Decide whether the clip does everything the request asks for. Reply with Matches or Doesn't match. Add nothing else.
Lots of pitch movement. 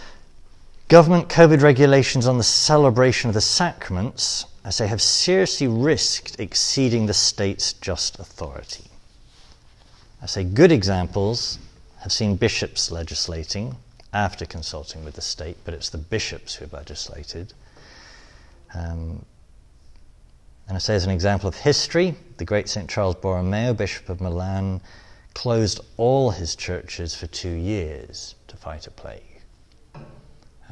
Matches